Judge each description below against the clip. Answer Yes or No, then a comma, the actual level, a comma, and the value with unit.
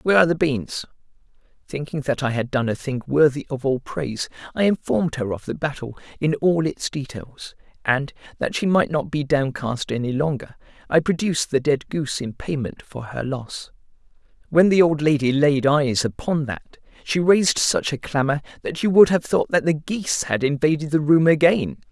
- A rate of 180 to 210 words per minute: Yes, average, 190 wpm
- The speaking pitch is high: No, medium, 145 Hz